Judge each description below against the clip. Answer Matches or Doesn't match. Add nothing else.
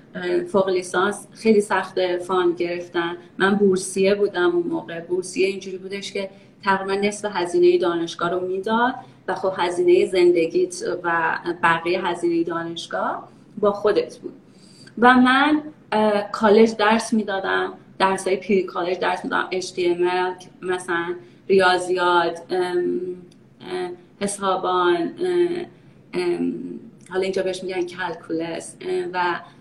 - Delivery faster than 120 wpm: Doesn't match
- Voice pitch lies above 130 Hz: Matches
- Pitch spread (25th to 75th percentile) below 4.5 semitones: Matches